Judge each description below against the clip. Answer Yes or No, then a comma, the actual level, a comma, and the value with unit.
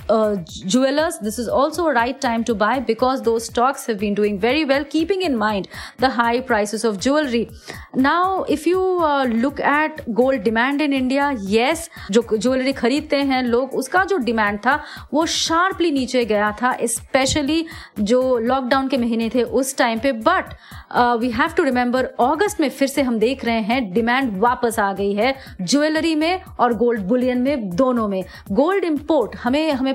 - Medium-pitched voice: No, very high, 255 Hz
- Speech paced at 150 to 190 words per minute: Yes, average, 165 wpm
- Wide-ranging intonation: No, average, 3.9 semitones